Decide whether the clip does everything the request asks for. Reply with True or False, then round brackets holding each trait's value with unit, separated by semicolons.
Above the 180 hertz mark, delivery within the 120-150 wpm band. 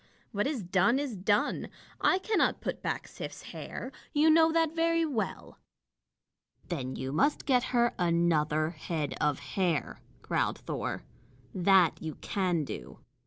True (190 Hz; 140 wpm)